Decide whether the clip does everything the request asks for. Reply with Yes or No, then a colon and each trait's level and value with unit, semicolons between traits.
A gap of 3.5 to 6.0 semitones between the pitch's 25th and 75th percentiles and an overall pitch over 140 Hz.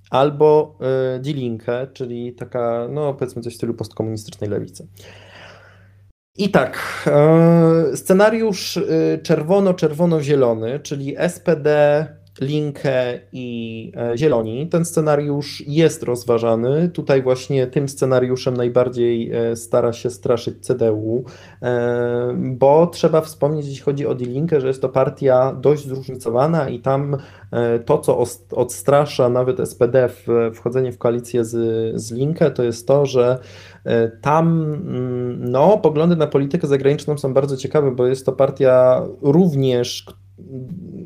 No: average, 3.9 semitones; low, 130 Hz